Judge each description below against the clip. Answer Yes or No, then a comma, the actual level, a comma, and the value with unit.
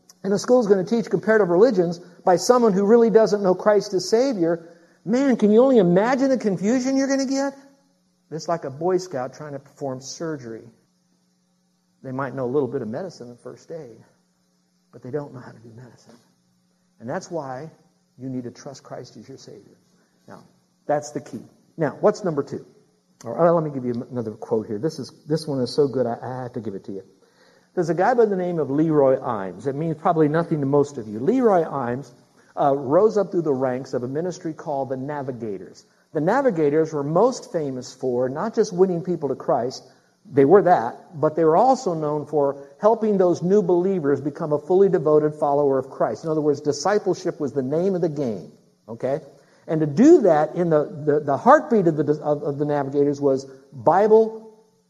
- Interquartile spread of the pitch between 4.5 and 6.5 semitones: Yes, average, 5.3 semitones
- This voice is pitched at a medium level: Yes, medium, 155 Hz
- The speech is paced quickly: Yes, fast, 210 wpm